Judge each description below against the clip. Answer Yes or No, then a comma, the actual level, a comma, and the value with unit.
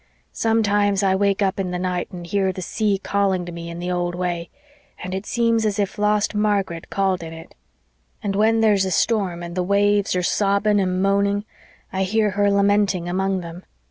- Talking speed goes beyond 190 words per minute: Yes, average, 200 wpm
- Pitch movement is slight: Yes, narrow, 2.1 semitones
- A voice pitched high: Yes, high, 195 Hz